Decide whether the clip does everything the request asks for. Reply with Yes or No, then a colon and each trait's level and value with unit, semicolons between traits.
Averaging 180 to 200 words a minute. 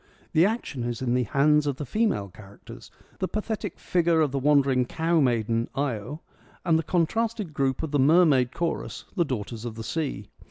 Yes: average, 185 wpm